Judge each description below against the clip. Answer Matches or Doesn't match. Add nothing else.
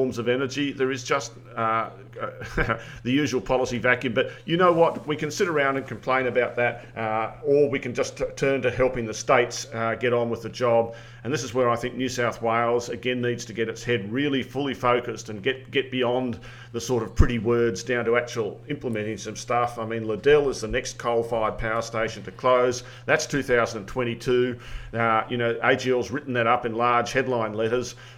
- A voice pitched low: Matches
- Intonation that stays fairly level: Matches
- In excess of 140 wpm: Matches